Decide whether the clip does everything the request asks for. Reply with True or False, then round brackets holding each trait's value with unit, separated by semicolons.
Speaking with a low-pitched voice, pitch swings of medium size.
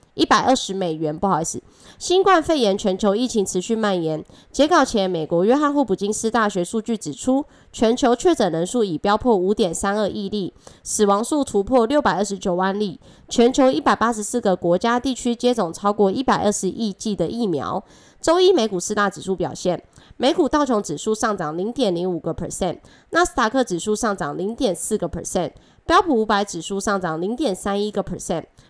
False (210 Hz; 4.7 semitones)